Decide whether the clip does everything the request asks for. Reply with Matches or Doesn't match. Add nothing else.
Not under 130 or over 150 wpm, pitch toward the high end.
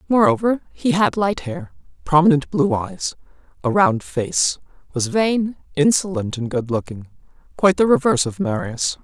Matches